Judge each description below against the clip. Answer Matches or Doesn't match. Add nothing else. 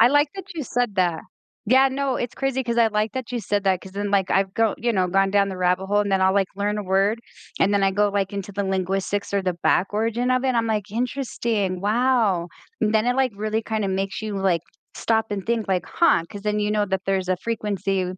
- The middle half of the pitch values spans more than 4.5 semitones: Doesn't match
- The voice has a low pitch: Doesn't match